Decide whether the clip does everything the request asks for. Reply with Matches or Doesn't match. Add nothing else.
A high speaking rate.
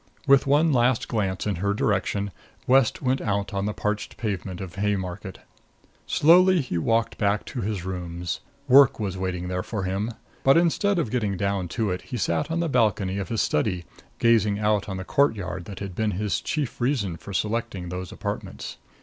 Doesn't match